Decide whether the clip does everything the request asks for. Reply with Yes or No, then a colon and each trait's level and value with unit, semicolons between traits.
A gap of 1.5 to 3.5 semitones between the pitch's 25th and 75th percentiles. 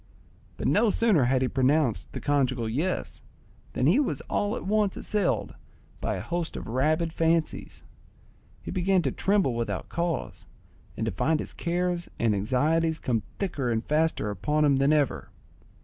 No: wide, 5.5 semitones